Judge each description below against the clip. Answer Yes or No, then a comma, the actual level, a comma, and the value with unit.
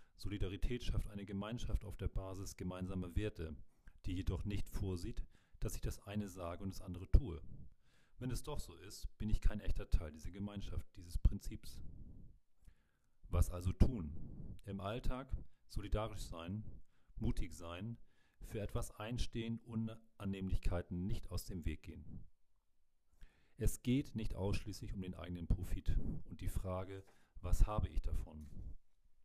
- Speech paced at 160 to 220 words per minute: No, average, 145 wpm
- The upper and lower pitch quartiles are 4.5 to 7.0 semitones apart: No, average, 3.5 semitones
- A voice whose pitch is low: Yes, very low, 95 Hz